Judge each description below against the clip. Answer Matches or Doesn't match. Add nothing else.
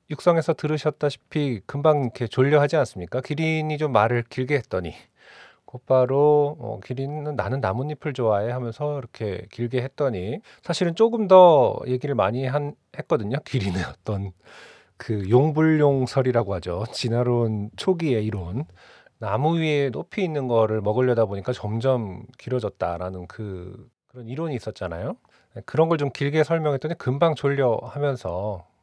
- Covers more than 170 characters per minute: Matches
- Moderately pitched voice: Doesn't match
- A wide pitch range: Doesn't match